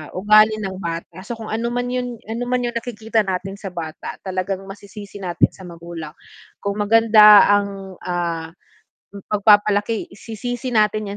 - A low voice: No, high, 205 Hz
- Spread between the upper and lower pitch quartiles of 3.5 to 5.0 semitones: No, average, 3.0 semitones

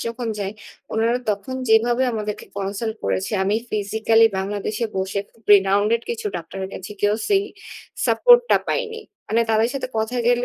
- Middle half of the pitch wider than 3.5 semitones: No, average, 2.7 semitones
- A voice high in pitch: Yes, high, 220 Hz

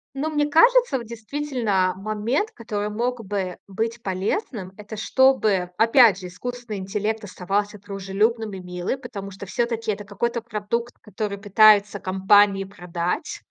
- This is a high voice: Yes, high, 210 Hz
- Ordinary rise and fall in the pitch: Yes, average, 3.3 semitones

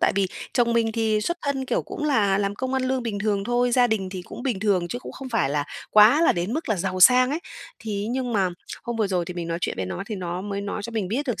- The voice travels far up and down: No, average, 4.3 semitones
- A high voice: Yes, high, 215 Hz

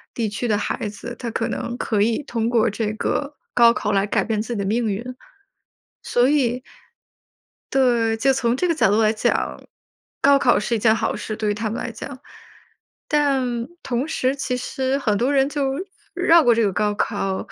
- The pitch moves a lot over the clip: No, average, 3.5 semitones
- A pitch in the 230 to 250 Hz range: Yes, high, 235 Hz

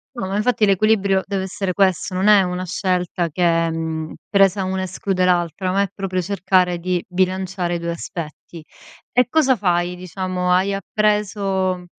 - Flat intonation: Yes, narrow, 1.8 semitones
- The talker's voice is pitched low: No, medium, 185 Hz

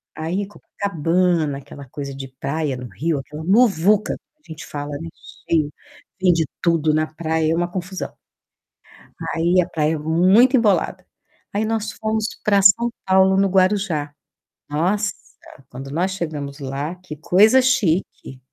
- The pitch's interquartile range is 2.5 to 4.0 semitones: No, average, 4.5 semitones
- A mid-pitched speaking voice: Yes, medium, 170 Hz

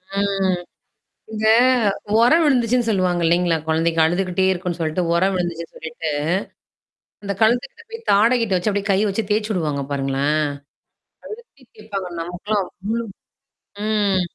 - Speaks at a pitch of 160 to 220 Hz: Yes, high, 195 Hz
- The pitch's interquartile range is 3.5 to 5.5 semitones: Yes, average, 3.9 semitones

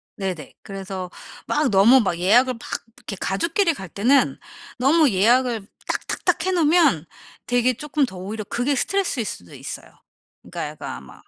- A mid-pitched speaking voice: No, high, 240 Hz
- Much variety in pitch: Yes, wide, 6.6 semitones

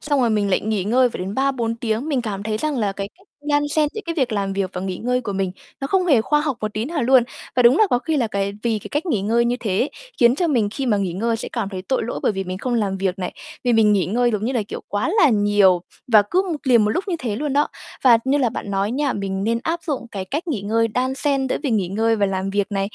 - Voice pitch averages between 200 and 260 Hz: Yes, high, 230 Hz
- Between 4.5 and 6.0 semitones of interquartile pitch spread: Yes, average, 4.9 semitones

